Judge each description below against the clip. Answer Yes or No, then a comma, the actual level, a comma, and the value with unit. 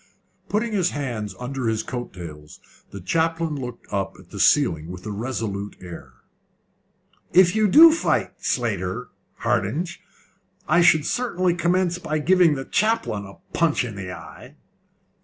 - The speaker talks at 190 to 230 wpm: No, average, 145 wpm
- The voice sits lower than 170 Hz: Yes, low, 135 Hz